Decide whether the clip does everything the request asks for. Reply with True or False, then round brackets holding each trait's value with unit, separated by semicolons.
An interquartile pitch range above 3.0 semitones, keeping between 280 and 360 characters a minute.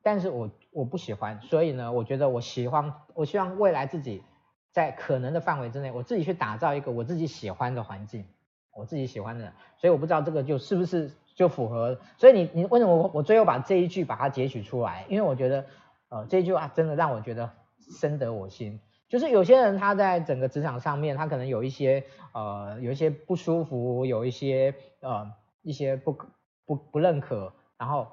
True (5.5 semitones; 320 characters per minute)